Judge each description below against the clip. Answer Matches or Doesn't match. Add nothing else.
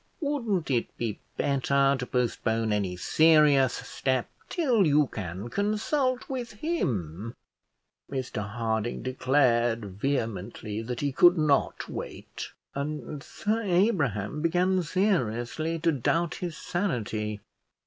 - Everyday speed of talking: Doesn't match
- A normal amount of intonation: Doesn't match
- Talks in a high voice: Doesn't match